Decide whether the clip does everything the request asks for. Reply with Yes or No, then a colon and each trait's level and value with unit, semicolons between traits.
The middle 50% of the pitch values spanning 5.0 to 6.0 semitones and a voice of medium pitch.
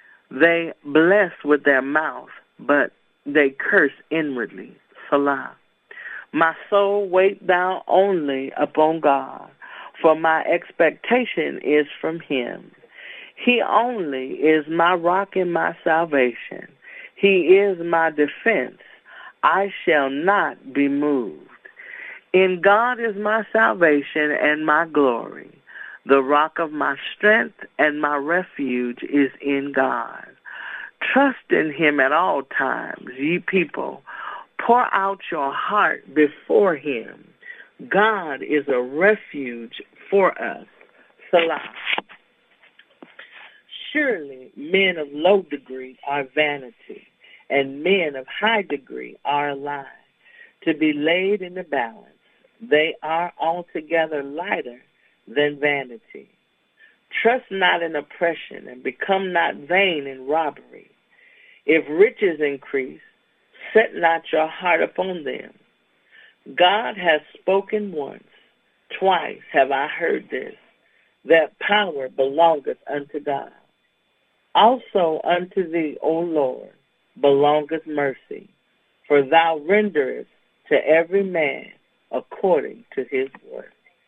Yes: wide, 5.4 semitones; medium, 165 Hz